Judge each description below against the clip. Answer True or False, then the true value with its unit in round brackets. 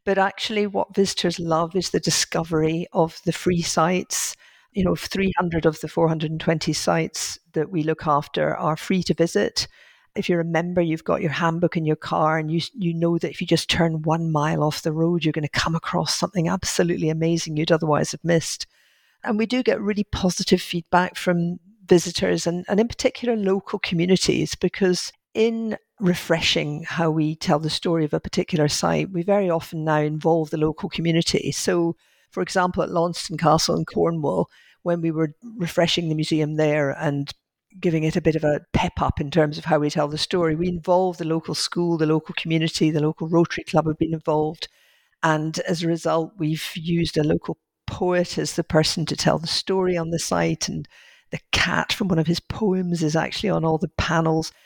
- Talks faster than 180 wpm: True (195 wpm)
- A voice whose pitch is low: False (165 Hz)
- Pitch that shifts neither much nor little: False (2.3 semitones)